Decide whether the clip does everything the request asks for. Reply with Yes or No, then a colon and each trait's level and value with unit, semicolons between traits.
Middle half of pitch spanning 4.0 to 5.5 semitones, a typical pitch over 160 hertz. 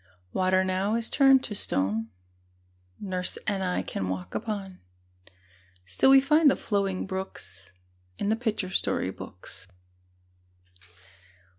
No: average, 3.5 semitones; high, 190 Hz